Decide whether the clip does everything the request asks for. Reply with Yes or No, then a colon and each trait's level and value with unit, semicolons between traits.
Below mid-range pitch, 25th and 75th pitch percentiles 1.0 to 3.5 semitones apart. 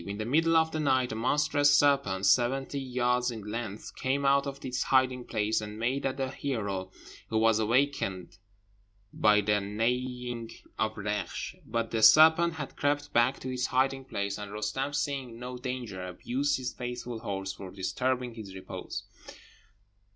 No: low, 125 Hz; average, 4.1 semitones